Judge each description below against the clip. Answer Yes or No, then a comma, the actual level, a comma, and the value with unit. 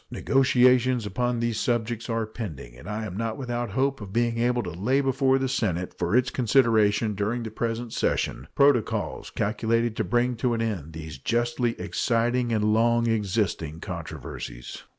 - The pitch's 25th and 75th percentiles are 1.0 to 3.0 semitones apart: Yes, narrow, 2.6 semitones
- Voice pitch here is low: Yes, low, 115 Hz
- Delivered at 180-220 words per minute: No, average, 165 wpm